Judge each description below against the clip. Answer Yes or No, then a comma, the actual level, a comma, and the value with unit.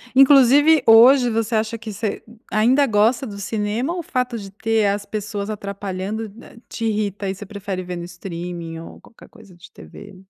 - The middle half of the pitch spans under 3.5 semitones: Yes, average, 2.8 semitones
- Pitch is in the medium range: No, high, 215 Hz